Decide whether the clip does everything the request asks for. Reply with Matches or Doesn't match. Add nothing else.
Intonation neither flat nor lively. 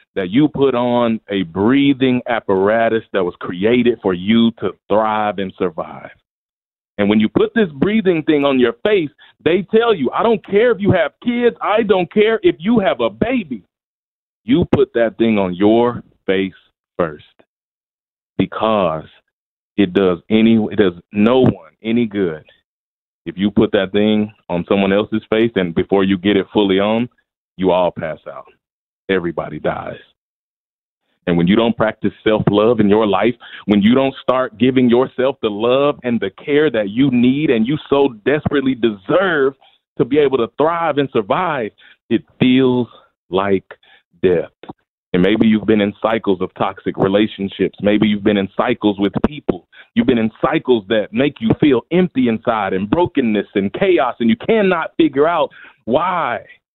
Doesn't match